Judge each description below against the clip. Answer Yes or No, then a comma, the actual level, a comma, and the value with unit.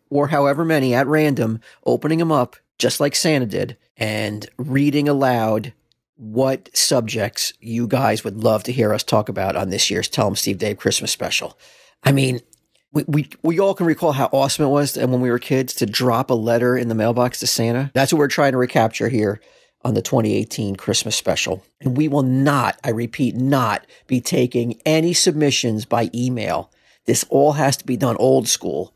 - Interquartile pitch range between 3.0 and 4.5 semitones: Yes, average, 3.5 semitones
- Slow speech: No, average, 195 wpm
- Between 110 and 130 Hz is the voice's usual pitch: Yes, low, 125 Hz